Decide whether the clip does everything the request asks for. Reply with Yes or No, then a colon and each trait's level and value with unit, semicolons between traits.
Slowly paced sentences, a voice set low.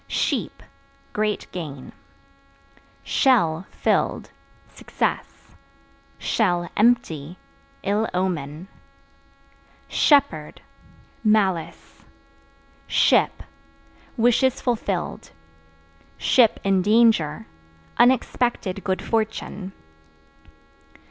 No: slow, 55 wpm; high, 200 Hz